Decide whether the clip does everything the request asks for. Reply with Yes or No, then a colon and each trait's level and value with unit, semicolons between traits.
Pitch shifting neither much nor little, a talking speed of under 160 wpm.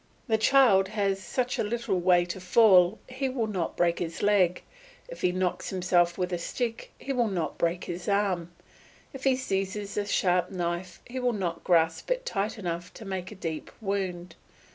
No: average, 3.9 semitones; average, 185 wpm